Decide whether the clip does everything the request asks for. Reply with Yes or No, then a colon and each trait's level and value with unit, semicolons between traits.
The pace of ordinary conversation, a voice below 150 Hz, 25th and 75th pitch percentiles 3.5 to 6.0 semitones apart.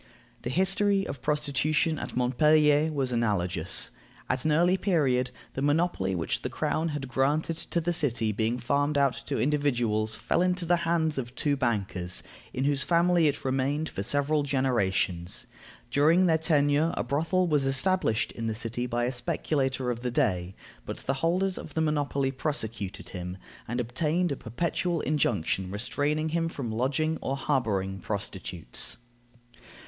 Yes: average, 155 wpm; medium, 140 Hz; average, 5.1 semitones